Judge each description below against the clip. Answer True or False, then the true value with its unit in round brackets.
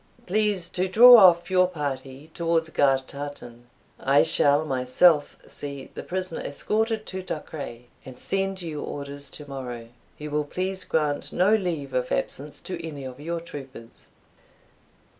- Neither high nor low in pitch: True (150 Hz)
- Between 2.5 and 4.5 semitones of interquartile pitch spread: False (4.9 semitones)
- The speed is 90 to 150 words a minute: True (140 wpm)